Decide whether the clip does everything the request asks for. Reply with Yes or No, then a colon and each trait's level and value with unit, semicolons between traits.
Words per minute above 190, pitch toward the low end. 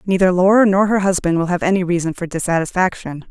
No: average, 200 wpm; medium, 180 Hz